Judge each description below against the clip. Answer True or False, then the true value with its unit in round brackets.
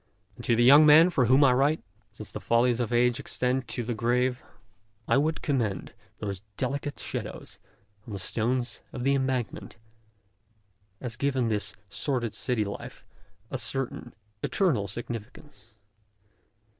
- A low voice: True (125 Hz)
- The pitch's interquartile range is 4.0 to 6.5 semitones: False (2.8 semitones)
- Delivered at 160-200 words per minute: False (145 wpm)